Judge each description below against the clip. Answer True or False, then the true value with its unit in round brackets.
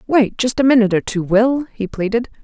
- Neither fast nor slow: False (220 wpm)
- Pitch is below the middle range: False (230 Hz)